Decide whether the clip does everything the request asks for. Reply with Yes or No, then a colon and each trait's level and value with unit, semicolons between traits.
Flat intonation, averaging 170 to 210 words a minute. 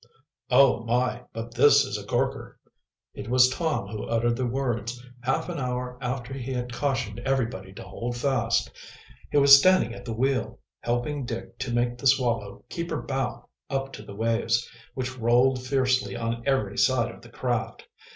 Yes: narrow, 2.2 semitones; average, 175 wpm